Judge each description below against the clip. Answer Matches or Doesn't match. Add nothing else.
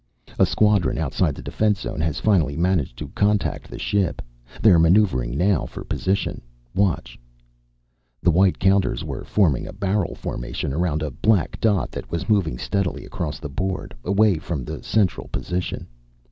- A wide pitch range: Doesn't match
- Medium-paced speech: Matches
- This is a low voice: Matches